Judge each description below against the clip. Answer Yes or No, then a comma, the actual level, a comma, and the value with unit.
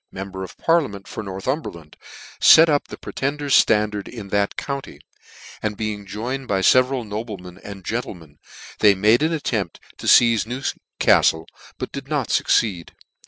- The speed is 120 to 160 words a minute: Yes, average, 150 wpm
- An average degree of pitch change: Yes, average, 4.8 semitones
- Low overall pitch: Yes, low, 105 Hz